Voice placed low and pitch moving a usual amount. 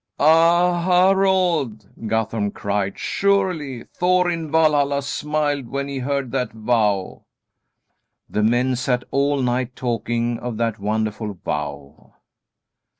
No: low, 130 Hz; wide, 6.0 semitones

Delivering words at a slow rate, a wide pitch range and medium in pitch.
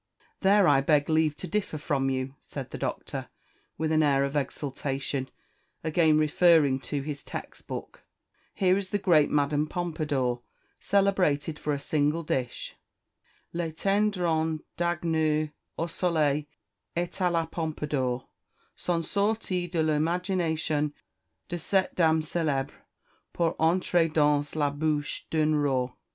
No: slow, 130 wpm; average, 3.0 semitones; medium, 155 Hz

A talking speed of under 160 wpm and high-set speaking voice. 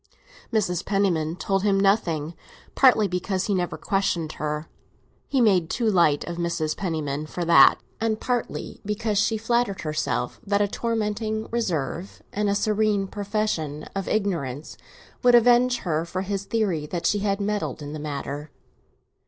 Yes: average, 145 wpm; high, 195 Hz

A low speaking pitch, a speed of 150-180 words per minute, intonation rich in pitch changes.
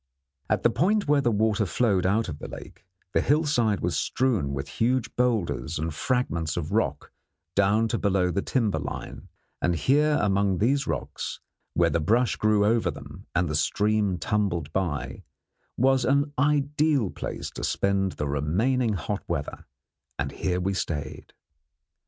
Yes: low, 105 Hz; average, 160 wpm; wide, 6.1 semitones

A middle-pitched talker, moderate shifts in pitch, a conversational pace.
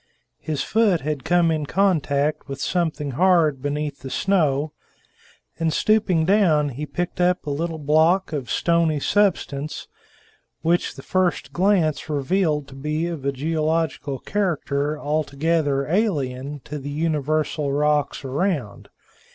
No: medium, 155 Hz; average, 3.2 semitones; slow, 130 wpm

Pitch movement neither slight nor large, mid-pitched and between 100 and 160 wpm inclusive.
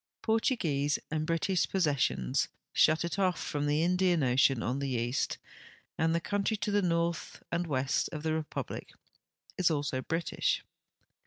Yes: average, 3.9 semitones; medium, 160 Hz; average, 150 wpm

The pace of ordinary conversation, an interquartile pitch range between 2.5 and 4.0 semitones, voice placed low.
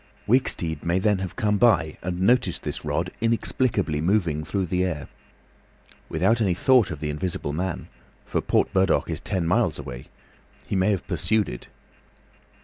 No: average, 150 wpm; average, 4.4 semitones; very low, 95 Hz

